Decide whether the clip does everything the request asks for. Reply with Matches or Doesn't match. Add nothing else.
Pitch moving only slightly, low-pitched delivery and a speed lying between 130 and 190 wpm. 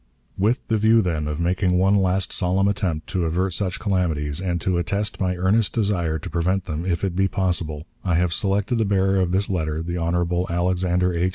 Doesn't match